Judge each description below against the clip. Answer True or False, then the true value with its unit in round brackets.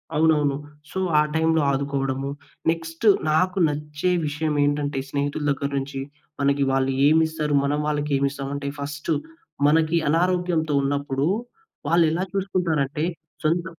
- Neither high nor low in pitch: True (150 Hz)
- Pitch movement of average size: False (2.3 semitones)